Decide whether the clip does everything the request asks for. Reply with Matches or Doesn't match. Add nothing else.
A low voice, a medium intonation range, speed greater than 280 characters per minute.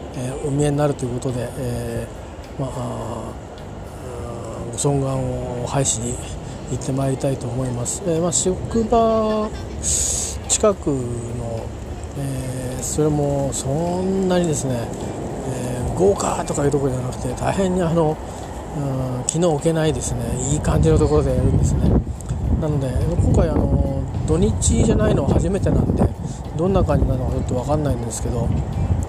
Matches